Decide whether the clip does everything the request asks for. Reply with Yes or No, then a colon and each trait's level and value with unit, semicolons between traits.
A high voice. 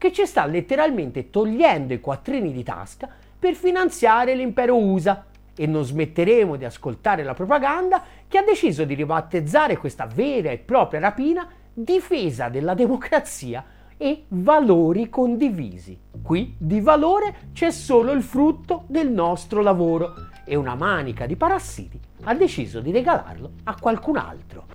Yes: high, 220 Hz